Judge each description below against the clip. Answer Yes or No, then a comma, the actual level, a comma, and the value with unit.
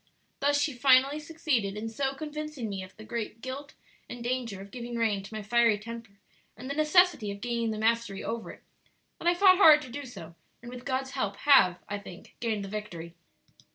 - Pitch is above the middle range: Yes, high, 235 Hz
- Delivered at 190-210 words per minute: Yes, fast, 205 wpm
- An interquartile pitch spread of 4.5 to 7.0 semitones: Yes, average, 4.8 semitones